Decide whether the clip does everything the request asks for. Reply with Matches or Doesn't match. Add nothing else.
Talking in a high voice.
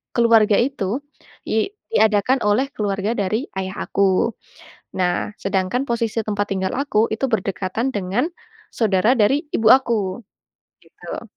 Matches